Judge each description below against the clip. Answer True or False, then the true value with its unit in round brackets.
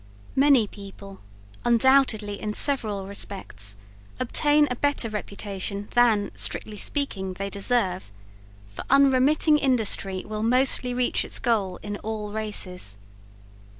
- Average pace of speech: False (115 wpm)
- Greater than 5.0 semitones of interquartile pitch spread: False (4.3 semitones)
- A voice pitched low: False (215 Hz)